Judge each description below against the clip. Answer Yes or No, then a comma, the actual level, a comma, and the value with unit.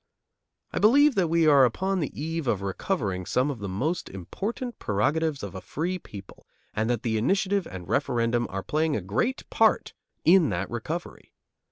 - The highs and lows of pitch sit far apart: Yes, wide, 8.9 semitones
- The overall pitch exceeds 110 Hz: Yes, medium, 140 Hz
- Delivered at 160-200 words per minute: Yes, average, 175 wpm